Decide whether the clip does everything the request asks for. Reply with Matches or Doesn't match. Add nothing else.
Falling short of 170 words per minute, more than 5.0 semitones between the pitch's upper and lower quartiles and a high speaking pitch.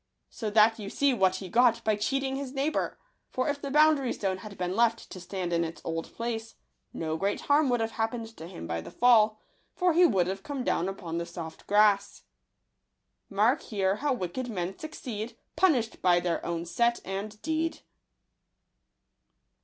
Doesn't match